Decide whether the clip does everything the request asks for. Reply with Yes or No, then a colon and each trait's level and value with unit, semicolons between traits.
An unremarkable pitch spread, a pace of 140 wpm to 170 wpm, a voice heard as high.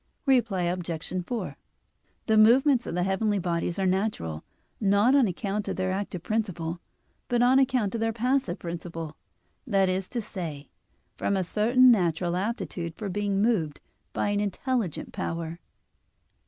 Yes: average, 4.5 semitones; average, 150 wpm; high, 195 Hz